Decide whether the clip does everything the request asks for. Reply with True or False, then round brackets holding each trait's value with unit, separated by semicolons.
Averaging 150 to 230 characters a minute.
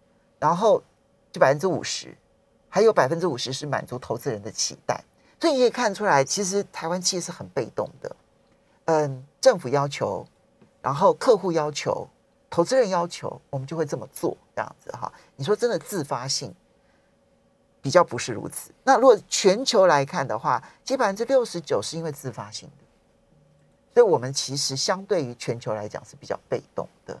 False (275 characters per minute)